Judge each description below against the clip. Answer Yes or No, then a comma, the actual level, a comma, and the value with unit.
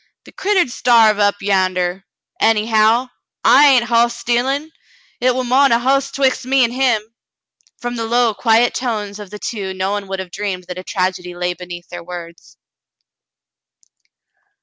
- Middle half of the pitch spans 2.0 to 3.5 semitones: No, average, 4.6 semitones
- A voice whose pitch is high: Yes, high, 220 Hz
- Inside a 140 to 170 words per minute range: Yes, average, 165 wpm